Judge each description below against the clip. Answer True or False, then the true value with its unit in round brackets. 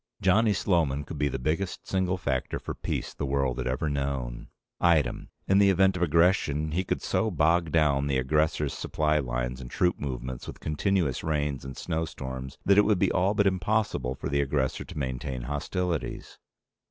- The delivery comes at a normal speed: True (180 wpm)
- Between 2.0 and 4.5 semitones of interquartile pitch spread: False (5.3 semitones)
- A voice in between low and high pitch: False (75 Hz)